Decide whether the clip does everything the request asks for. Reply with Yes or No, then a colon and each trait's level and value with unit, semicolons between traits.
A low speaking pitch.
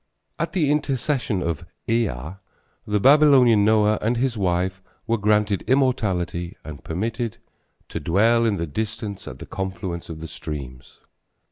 Yes: low, 105 Hz